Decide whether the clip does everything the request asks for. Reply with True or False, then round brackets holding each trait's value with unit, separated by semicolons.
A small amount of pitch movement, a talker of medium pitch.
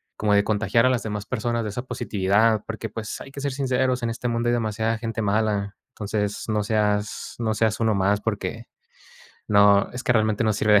False (2.1 semitones; 110 Hz)